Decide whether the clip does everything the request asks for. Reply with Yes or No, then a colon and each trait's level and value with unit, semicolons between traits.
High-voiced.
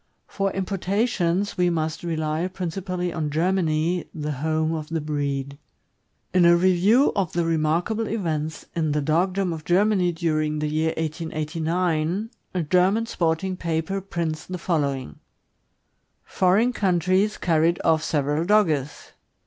No: medium, 170 Hz